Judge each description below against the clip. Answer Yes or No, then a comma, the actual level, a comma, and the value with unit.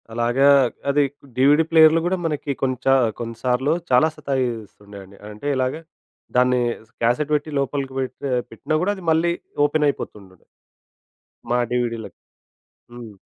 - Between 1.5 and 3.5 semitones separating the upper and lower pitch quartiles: No, average, 3.9 semitones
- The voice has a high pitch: No, low, 130 Hz